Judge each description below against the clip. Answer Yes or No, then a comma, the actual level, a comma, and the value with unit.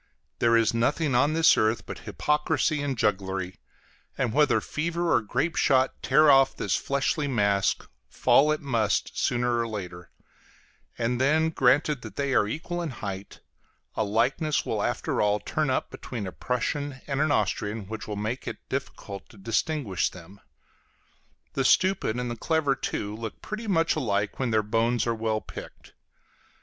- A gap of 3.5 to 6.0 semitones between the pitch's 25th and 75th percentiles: Yes, wide, 5.5 semitones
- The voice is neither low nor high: No, low, 125 Hz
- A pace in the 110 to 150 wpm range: No, average, 165 wpm